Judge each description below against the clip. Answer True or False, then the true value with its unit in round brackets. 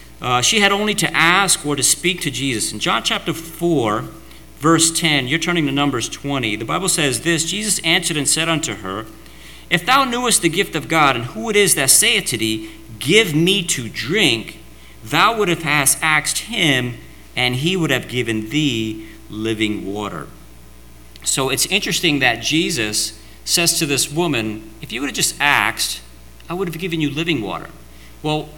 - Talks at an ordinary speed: True (180 wpm)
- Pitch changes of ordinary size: False (7.3 semitones)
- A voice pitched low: False (150 Hz)